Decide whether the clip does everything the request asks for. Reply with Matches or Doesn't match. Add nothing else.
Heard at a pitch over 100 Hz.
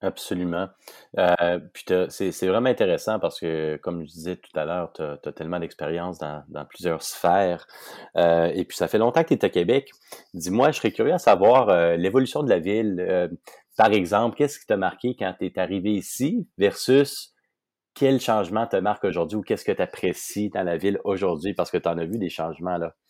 Doesn't match